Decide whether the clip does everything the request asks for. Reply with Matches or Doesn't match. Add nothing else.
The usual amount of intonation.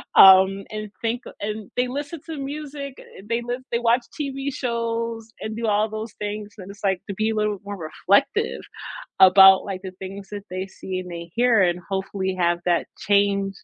Matches